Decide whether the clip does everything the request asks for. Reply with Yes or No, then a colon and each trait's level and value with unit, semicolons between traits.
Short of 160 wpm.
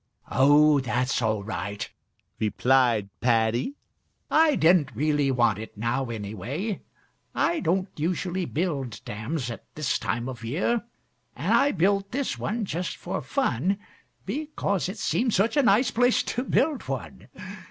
Yes: average, 140 wpm